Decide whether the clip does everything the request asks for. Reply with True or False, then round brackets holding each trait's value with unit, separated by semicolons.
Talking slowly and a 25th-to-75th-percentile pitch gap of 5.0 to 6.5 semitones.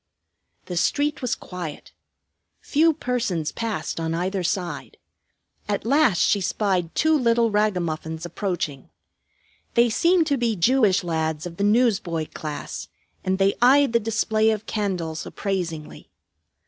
True (130 wpm; 5.5 semitones)